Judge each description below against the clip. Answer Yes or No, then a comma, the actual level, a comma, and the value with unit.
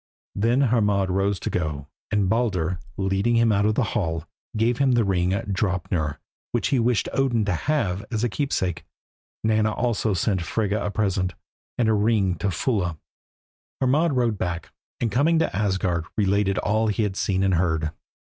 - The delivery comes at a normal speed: Yes, average, 170 wpm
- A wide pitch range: No, average, 3.8 semitones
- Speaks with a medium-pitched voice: No, low, 100 Hz